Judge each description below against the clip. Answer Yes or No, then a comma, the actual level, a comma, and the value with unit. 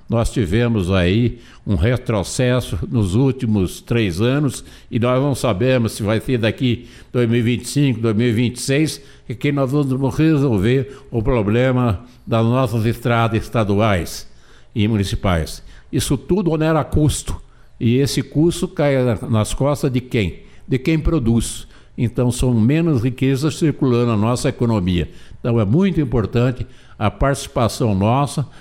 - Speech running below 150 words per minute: Yes, average, 130 wpm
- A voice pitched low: Yes, low, 125 Hz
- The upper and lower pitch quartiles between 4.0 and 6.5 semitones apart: No, average, 3.2 semitones